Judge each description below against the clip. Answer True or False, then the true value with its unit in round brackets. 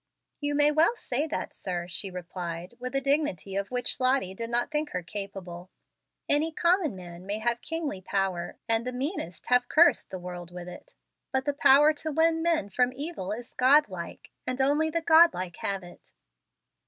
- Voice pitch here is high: True (245 Hz)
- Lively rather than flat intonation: True (8.2 semitones)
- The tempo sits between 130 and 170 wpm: False (180 wpm)